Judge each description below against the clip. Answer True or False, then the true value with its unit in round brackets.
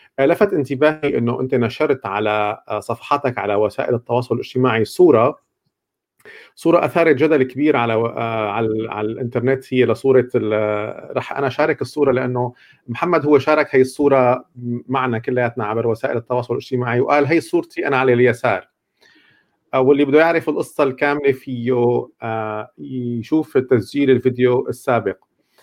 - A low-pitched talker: True (125 Hz)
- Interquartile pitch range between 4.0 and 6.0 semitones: False (3.5 semitones)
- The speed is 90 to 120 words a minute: False (135 wpm)